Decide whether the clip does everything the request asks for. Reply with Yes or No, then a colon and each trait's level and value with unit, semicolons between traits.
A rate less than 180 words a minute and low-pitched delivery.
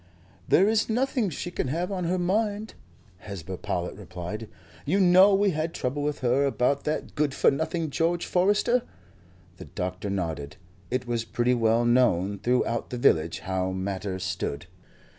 Yes: average, 160 wpm; low, 125 Hz